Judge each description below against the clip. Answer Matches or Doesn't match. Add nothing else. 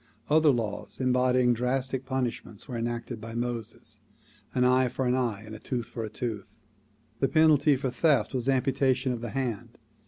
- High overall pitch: Doesn't match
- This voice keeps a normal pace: Matches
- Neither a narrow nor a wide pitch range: Doesn't match